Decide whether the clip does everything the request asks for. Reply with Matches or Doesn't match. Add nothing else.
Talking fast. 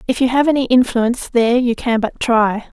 Matches